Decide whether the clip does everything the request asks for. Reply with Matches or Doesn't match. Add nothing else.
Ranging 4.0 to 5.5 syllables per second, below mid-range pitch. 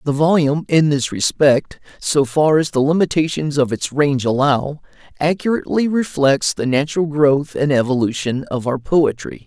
Doesn't match